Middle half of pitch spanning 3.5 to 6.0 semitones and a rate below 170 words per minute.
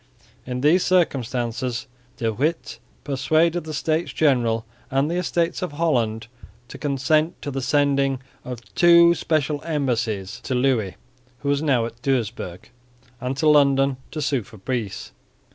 Yes: average, 4.2 semitones; average, 145 wpm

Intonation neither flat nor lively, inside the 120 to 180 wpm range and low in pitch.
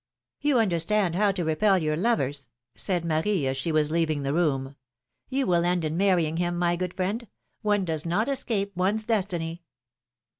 No: average, 4.3 semitones; average, 175 wpm; medium, 175 Hz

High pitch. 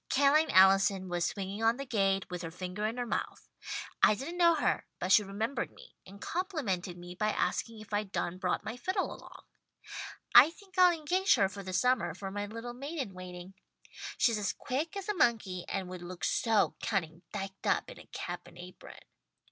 Yes: high, 210 Hz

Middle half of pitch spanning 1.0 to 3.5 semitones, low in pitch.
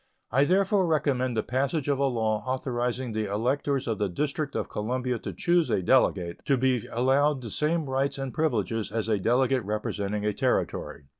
No: average, 4.2 semitones; low, 130 Hz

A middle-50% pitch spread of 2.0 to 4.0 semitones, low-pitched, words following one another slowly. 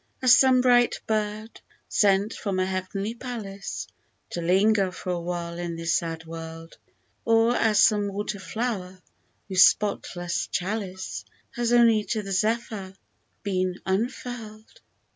No: average, 3.4 semitones; high, 200 Hz; slow, 130 wpm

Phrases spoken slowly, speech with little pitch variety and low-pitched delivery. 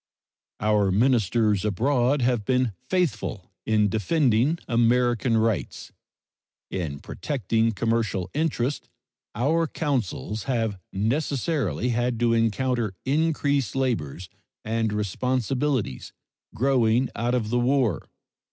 No: slow, 95 wpm; average, 3.8 semitones; low, 120 Hz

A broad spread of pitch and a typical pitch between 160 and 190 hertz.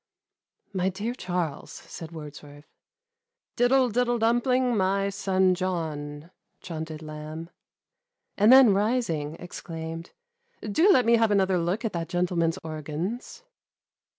Yes: wide, 6.2 semitones; medium, 185 Hz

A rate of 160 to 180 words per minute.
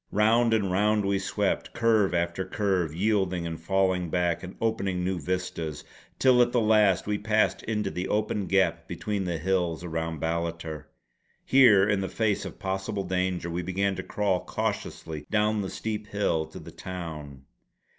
Yes: average, 165 wpm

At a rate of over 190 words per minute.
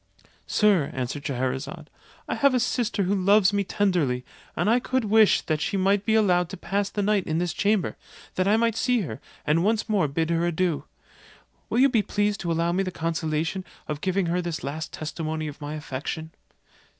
Yes: average, 200 wpm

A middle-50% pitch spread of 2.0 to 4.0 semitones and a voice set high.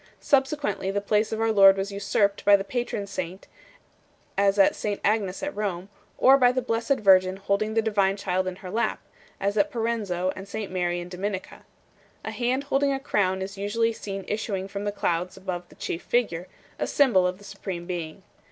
Yes: average, 2.9 semitones; high, 200 Hz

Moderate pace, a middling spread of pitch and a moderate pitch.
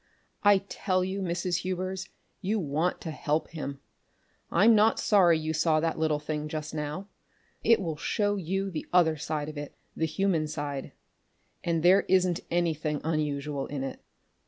Yes: average, 160 wpm; average, 3.6 semitones; medium, 165 Hz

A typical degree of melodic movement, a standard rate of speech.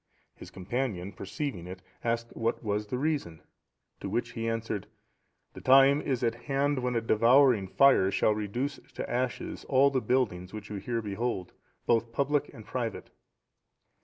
Yes: average, 4.0 semitones; average, 160 wpm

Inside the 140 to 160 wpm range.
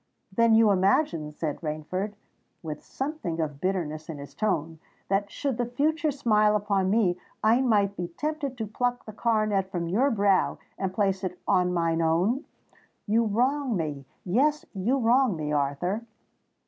Yes: average, 155 wpm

